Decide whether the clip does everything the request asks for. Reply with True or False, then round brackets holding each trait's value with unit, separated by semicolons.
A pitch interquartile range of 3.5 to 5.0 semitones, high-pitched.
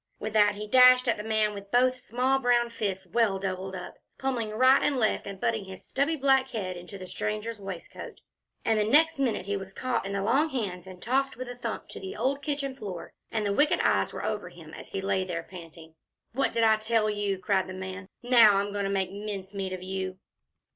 True (4.6 semitones; 210 Hz)